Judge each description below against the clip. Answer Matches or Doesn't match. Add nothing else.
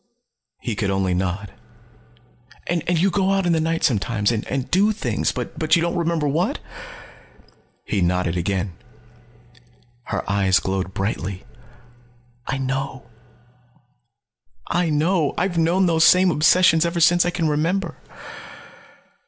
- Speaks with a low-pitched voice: Doesn't match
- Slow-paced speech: Matches